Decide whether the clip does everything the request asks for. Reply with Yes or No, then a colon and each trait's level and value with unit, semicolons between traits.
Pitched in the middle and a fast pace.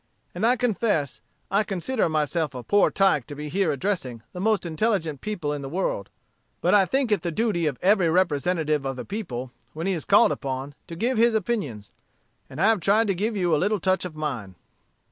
Yes: medium, 175 Hz; fast, 210 wpm